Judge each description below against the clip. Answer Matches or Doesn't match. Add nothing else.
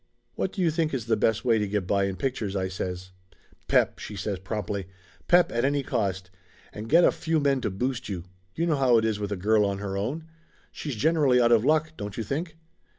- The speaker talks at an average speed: Doesn't match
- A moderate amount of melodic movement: Doesn't match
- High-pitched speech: Doesn't match